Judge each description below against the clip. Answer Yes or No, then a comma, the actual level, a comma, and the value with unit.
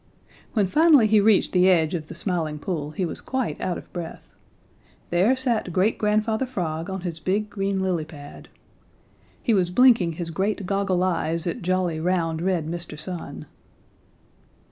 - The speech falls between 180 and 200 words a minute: No, average, 165 wpm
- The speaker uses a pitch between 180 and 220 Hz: Yes, medium, 185 Hz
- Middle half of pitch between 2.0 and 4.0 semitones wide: Yes, average, 3.7 semitones